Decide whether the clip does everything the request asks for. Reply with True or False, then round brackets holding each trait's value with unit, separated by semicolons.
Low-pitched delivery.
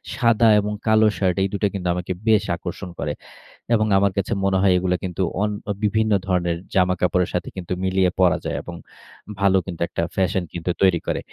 True (95 Hz)